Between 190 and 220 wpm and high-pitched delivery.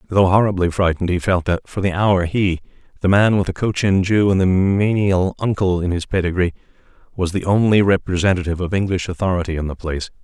No: average, 195 wpm; very low, 95 Hz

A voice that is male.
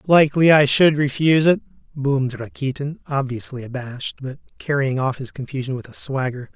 Yes: male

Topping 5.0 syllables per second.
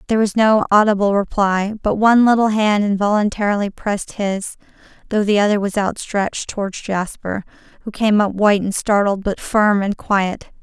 Yes: 5.2 syllables/s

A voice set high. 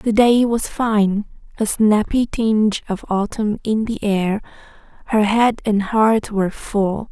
Yes: high, 215 Hz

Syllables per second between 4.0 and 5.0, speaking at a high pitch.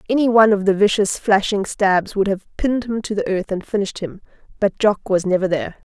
No: 6.0 syllables/s; high, 205 Hz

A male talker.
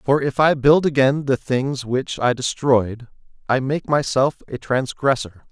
Yes: male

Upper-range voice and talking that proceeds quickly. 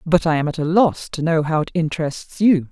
No: medium, 160 Hz; fast, 265 wpm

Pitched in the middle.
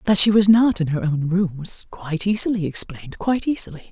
Yes: medium, 180 Hz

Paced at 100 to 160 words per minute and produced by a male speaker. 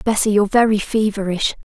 No: average, 140 wpm; female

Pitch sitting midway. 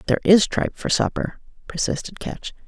No: high, 200 Hz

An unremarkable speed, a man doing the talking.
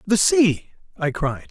Yes: average, 160 wpm; male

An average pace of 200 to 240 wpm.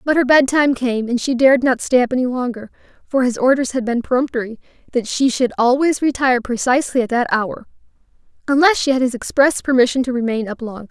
Yes: fast, 205 wpm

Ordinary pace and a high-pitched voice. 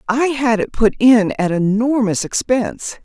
Yes: average, 160 wpm; high, 235 Hz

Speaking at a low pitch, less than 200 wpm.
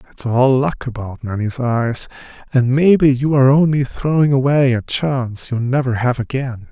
Yes: low, 130 Hz; average, 170 wpm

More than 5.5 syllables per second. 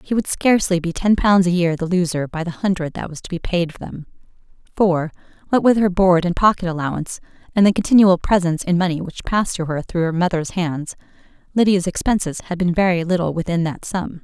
Yes: 5.8 syllables/s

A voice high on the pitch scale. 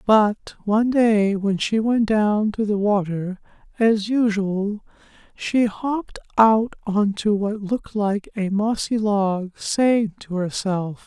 Yes: high, 210 Hz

